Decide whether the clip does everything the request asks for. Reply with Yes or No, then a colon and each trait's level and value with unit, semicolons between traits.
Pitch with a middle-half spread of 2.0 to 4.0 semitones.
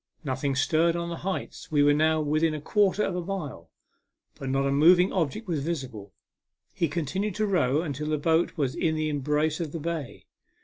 Yes: average, 3.0 semitones